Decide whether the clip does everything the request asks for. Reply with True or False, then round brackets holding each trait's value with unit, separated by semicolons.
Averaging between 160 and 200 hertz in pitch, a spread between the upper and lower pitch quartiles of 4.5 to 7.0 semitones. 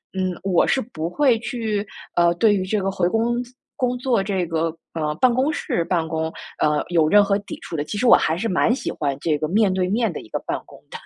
True (190 Hz; 5.5 semitones)